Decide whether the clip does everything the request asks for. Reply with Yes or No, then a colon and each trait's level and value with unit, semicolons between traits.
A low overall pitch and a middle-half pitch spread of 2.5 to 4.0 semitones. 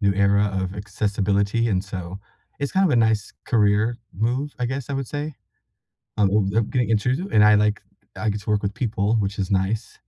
Yes: low, 105 Hz; average, 2.9 semitones